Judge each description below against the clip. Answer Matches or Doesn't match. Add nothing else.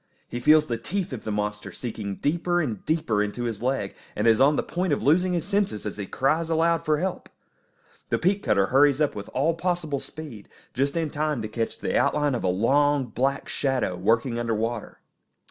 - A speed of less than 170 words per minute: Doesn't match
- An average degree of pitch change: Doesn't match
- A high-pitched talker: Doesn't match